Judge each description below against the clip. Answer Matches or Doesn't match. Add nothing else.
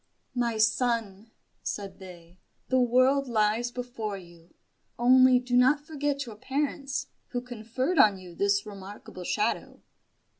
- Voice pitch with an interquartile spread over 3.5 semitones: Matches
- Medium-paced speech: Doesn't match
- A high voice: Matches